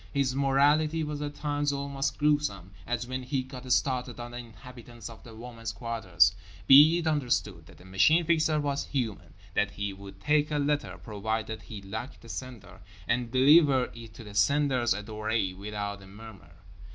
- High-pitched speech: No, low, 120 Hz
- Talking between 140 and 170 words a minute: Yes, average, 165 wpm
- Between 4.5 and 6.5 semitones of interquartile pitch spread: Yes, average, 5.2 semitones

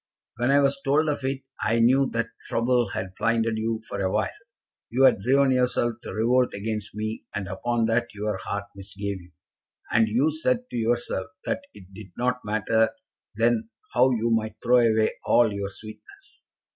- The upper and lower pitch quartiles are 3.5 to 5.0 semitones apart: No, average, 2.9 semitones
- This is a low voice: Yes, low, 115 Hz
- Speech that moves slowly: No, average, 175 wpm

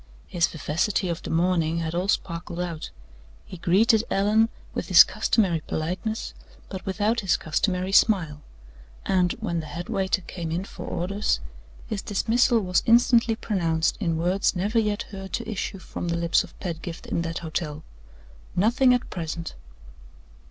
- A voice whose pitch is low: No, medium, 185 Hz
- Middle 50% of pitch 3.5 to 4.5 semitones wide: Yes, average, 3.9 semitones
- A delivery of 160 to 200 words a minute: No, average, 150 wpm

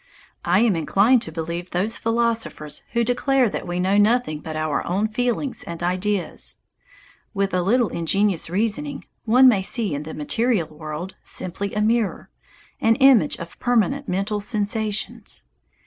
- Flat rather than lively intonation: No, average, 5.0 semitones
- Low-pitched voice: No, high, 205 Hz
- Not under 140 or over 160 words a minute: Yes, average, 150 wpm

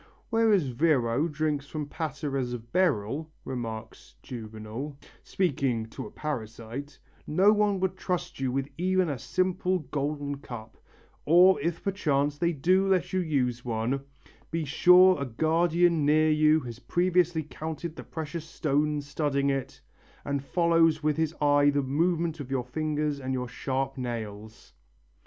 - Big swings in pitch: No, average, 4.2 semitones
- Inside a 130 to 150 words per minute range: Yes, average, 145 wpm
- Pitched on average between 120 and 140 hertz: No, medium, 150 Hz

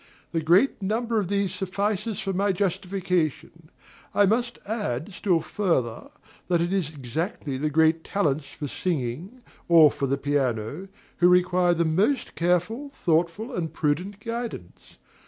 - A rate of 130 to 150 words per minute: Yes, average, 140 wpm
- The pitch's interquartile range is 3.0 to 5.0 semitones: Yes, average, 4.5 semitones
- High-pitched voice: No, medium, 180 Hz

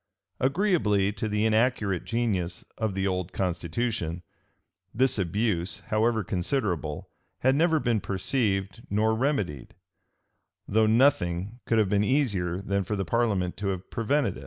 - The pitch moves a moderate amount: Yes, average, 4.1 semitones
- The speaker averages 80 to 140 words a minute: Yes, slow, 135 wpm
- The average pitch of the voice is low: Yes, low, 105 Hz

